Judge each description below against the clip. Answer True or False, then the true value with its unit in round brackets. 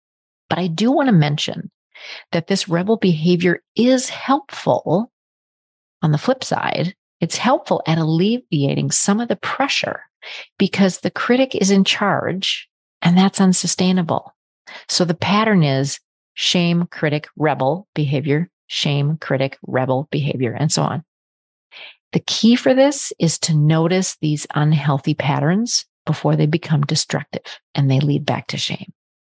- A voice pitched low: False (170 Hz)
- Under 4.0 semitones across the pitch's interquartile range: False (4.7 semitones)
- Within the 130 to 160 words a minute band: True (140 wpm)